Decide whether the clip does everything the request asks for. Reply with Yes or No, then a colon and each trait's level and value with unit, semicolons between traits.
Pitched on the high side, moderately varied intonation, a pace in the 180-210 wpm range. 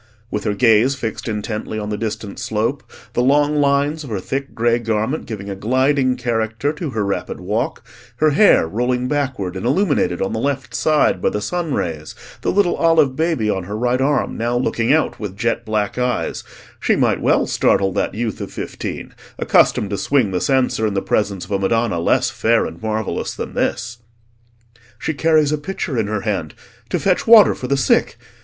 No: low, 120 Hz; average, 4.9 semitones; average, 190 wpm